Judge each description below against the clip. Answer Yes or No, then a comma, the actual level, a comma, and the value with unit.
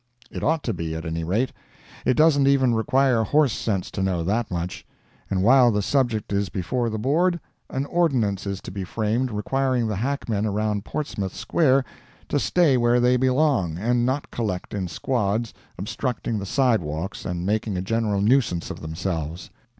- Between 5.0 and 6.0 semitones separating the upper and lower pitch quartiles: Yes, average, 5.3 semitones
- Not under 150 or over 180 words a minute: Yes, average, 175 wpm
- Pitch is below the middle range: Yes, low, 110 Hz